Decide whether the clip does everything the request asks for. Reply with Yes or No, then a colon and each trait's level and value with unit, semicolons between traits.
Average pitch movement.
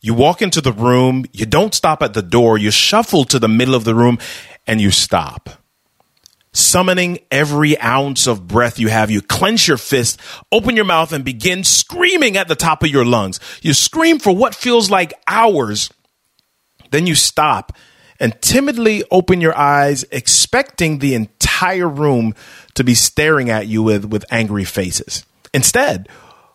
No: wide, 7.6 semitones